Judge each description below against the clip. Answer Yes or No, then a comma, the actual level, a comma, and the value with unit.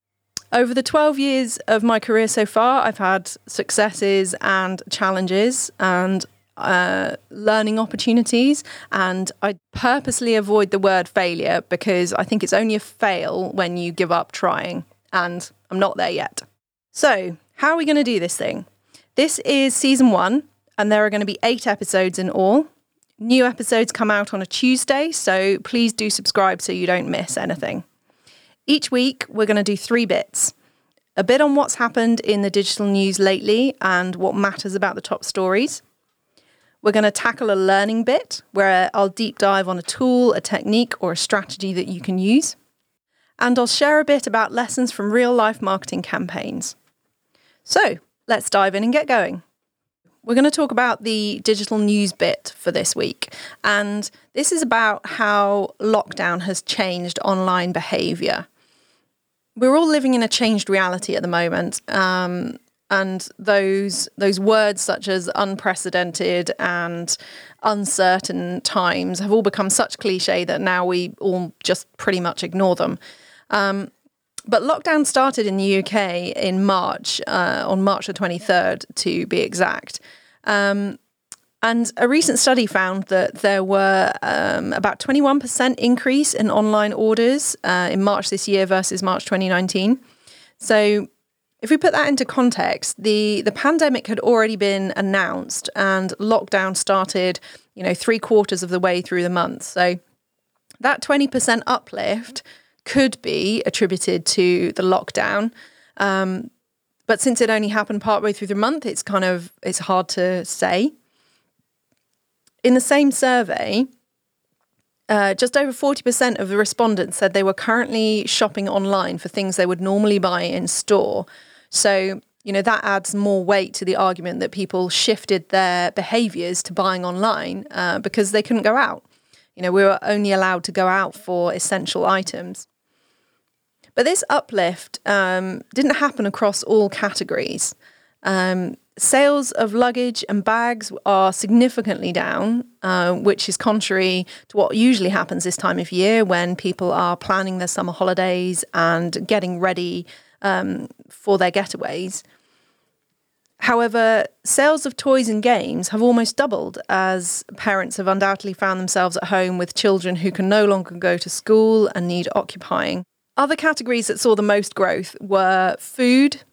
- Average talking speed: Yes, average, 160 wpm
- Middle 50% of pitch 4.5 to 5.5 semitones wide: No, average, 3.8 semitones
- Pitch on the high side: Yes, high, 205 Hz